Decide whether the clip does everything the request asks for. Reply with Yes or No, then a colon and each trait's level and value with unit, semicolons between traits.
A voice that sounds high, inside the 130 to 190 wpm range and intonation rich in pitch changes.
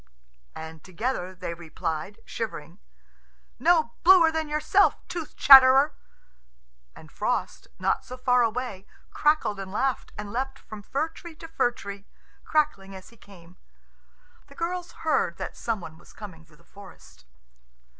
Yes: high, 230 Hz; average, 145 wpm; wide, 8.1 semitones